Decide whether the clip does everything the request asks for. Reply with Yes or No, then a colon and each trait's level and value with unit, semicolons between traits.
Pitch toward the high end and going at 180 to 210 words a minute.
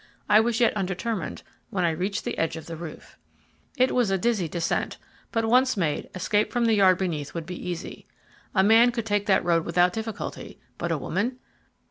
Yes: high, 195 Hz; average, 195 wpm